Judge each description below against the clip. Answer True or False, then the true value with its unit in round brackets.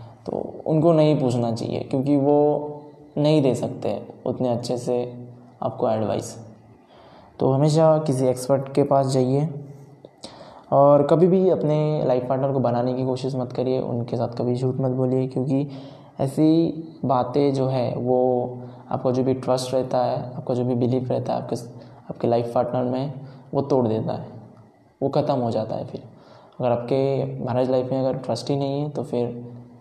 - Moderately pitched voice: False (130 Hz)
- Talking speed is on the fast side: False (170 wpm)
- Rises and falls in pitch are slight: True (2.3 semitones)